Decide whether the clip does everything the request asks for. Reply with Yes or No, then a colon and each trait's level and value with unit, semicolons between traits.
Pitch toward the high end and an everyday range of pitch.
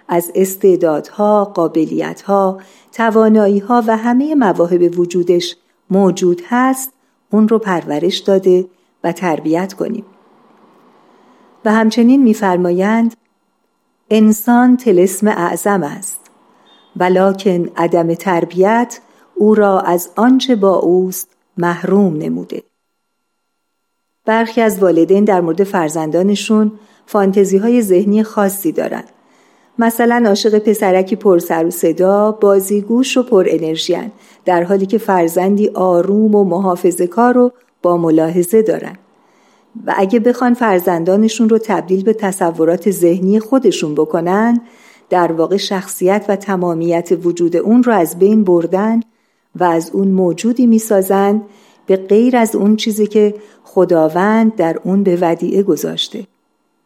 Yes: high, 195 Hz; average, 3.7 semitones